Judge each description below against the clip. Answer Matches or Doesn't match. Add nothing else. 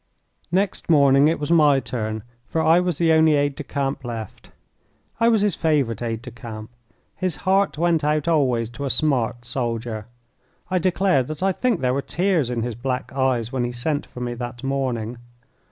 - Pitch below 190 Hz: Matches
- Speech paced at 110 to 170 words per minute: Doesn't match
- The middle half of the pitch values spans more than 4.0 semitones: Matches